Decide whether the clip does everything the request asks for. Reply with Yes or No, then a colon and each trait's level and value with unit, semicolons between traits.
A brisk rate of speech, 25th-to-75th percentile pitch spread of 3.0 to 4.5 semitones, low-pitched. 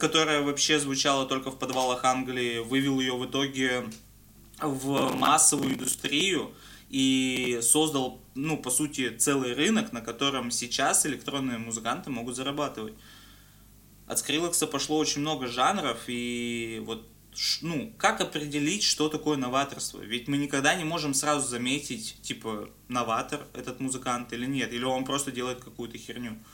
No: average, 140 wpm; average, 3.3 semitones; low, 130 Hz